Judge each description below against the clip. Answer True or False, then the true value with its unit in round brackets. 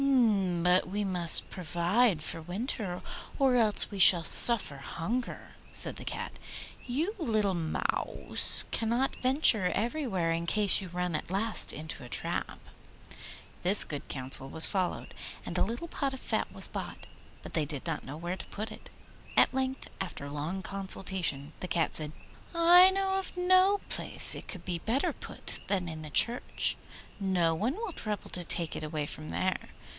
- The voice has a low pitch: False (190 Hz)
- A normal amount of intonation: False (6.6 semitones)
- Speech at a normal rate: True (170 wpm)